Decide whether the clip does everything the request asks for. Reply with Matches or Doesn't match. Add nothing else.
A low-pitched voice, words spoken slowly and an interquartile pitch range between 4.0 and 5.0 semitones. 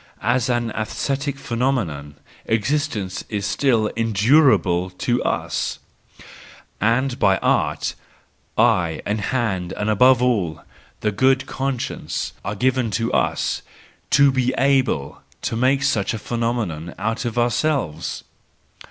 Matches